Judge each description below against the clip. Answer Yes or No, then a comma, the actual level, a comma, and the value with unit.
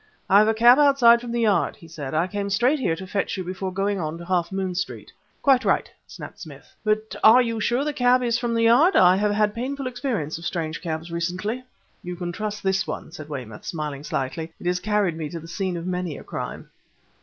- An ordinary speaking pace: No, fast, 235 wpm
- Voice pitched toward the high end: Yes, high, 195 Hz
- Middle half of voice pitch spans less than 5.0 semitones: No, wide, 5.4 semitones